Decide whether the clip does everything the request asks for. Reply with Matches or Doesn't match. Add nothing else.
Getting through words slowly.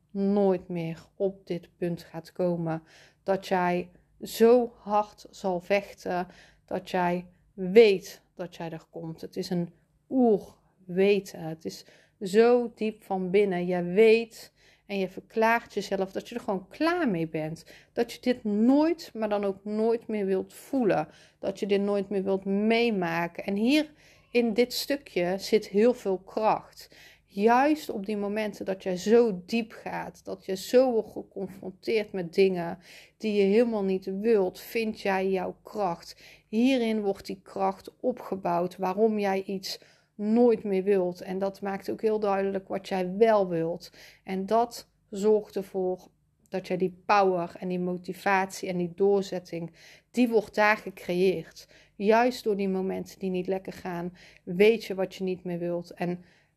Doesn't match